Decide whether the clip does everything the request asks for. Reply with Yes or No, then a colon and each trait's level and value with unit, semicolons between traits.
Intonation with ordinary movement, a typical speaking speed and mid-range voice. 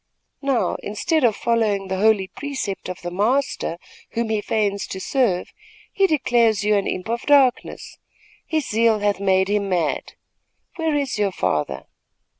No: average, 4.7 semitones; average, 155 wpm; high, 215 Hz